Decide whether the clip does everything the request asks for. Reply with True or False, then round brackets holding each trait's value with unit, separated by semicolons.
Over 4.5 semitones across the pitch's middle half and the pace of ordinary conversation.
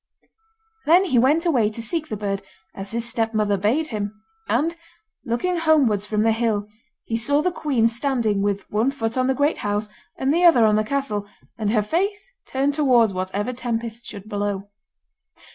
True (5.0 semitones; 180 wpm)